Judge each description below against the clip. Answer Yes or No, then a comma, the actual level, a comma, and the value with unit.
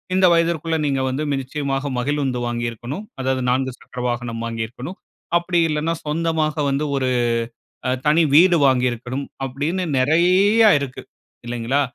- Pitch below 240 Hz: Yes, medium, 140 Hz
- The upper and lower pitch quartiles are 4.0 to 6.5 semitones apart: Yes, average, 4.5 semitones